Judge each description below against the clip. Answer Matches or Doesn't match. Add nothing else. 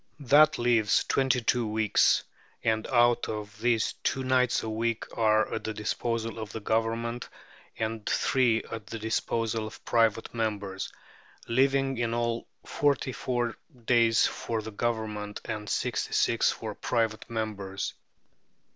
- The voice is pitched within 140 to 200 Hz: Doesn't match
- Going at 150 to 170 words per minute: Doesn't match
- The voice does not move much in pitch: Matches